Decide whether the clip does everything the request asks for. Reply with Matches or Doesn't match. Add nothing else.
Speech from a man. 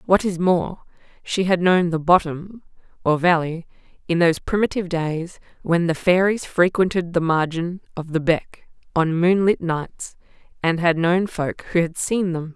Doesn't match